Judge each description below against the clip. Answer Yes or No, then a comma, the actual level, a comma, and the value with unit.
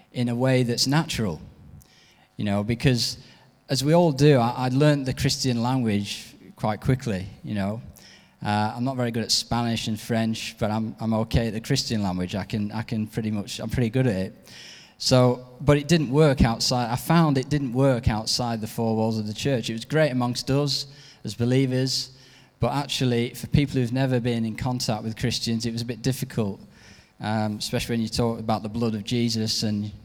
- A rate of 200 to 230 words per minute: Yes, fast, 205 wpm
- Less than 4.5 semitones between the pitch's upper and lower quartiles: Yes, average, 3.1 semitones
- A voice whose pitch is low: Yes, low, 120 Hz